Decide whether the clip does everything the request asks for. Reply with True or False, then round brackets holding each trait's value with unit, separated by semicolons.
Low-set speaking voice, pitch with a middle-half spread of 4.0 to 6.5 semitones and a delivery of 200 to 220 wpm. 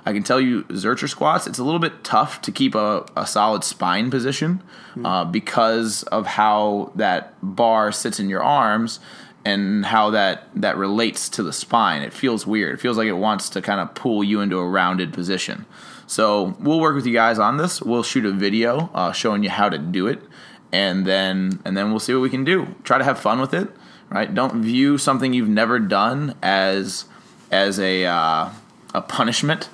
True (110 Hz; 4.3 semitones; 205 wpm)